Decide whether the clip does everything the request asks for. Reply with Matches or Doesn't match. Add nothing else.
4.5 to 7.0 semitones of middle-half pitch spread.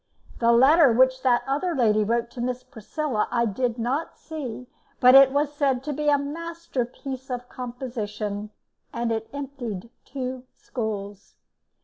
Doesn't match